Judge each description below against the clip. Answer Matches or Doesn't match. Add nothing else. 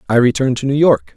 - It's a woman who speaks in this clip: Doesn't match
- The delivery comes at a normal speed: Doesn't match